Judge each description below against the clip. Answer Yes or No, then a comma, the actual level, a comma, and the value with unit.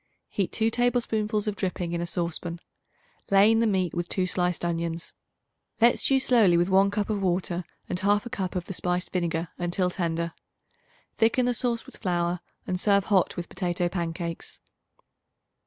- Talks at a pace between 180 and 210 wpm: No, average, 170 wpm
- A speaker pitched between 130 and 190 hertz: Yes, medium, 185 Hz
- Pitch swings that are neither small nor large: Yes, average, 3.3 semitones